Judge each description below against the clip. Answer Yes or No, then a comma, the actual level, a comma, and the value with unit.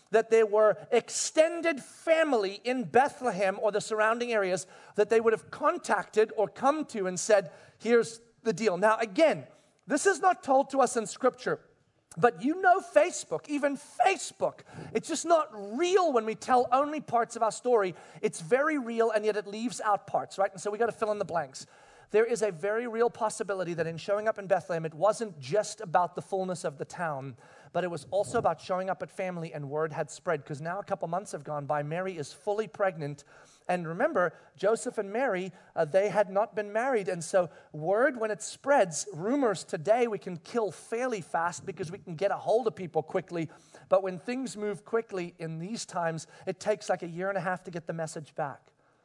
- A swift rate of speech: Yes, fast, 210 wpm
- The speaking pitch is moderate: No, high, 205 Hz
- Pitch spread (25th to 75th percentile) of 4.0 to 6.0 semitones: Yes, average, 4.5 semitones